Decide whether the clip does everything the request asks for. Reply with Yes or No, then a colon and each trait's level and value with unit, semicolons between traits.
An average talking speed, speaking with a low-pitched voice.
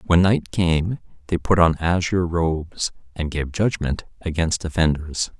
Yes: average, 145 wpm; very low, 85 Hz